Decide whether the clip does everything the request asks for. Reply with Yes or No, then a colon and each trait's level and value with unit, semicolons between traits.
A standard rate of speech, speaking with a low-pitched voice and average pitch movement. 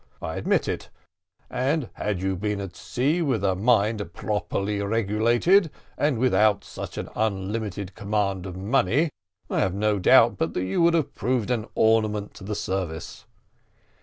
Yes: average, 165 wpm; low, 105 Hz; average, 3.6 semitones